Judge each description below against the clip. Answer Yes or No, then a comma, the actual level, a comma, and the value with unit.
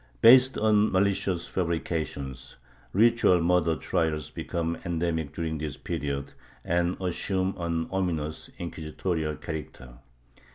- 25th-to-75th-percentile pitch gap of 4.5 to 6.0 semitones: No, average, 3.2 semitones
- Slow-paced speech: Yes, slow, 100 wpm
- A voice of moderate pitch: No, very low, 85 Hz